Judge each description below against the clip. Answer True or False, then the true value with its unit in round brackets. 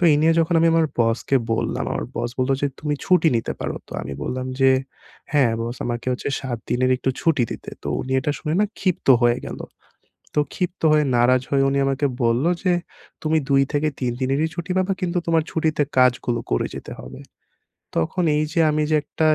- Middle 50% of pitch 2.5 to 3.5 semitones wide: False (4.4 semitones)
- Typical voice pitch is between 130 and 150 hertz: True (140 Hz)